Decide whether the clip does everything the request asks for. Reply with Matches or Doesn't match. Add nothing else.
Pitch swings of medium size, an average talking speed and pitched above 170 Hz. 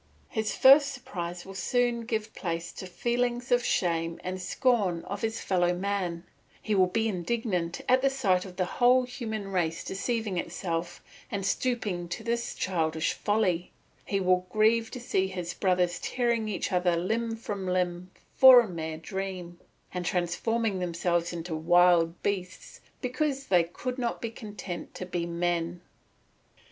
Matches